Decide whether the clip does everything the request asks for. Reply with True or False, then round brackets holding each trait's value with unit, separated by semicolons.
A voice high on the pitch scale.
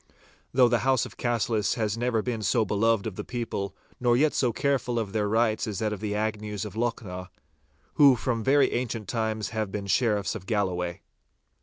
False (110 Hz)